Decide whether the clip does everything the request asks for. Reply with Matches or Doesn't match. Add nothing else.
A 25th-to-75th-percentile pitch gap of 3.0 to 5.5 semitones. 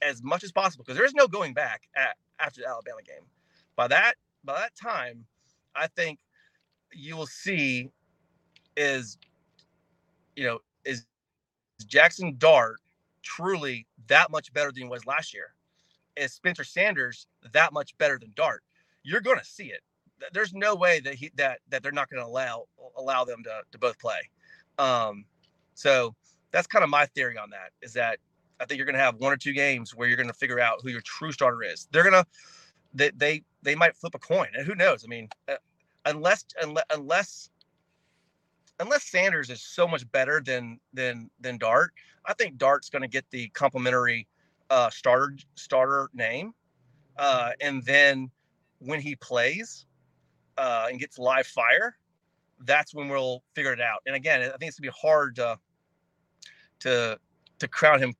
Matches